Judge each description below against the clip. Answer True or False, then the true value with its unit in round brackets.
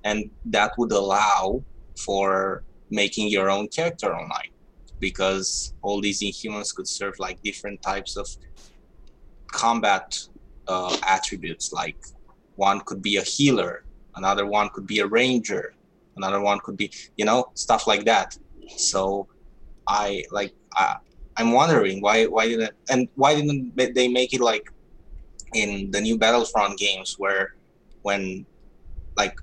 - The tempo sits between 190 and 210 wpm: False (140 wpm)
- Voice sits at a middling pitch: False (100 Hz)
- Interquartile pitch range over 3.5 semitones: False (2.8 semitones)